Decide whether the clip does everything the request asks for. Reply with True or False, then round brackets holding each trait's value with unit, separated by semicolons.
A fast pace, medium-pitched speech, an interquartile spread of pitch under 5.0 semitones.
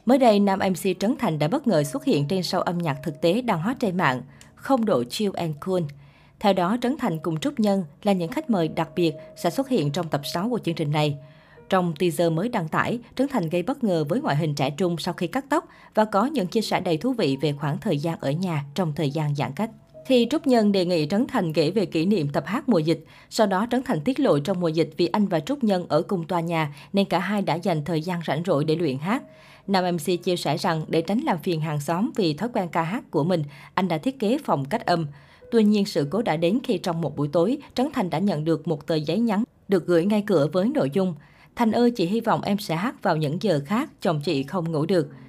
False (265 wpm; 180 Hz; 5.3 semitones)